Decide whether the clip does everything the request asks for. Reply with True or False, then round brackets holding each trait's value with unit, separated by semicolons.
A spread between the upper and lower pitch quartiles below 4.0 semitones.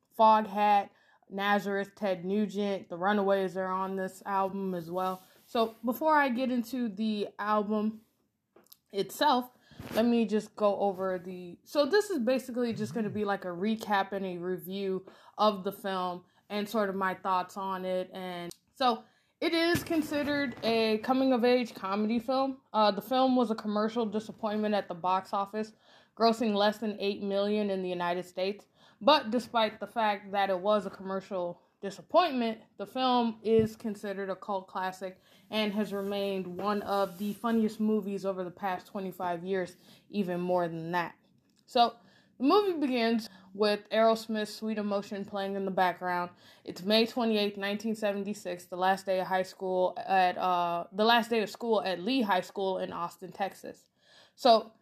True (2.9 semitones)